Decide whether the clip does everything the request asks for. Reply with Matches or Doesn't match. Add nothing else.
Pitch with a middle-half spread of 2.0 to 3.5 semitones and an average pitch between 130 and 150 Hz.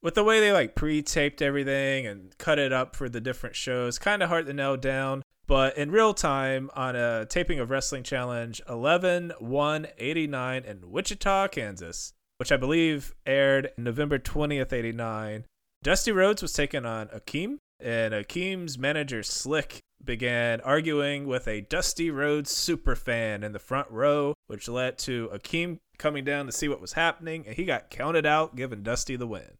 Doesn't match